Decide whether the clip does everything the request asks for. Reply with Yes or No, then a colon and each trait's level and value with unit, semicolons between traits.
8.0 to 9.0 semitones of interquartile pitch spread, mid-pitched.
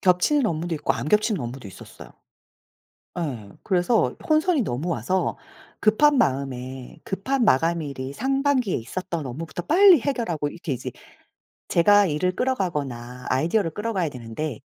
Yes: wide, 8.4 semitones; medium, 170 Hz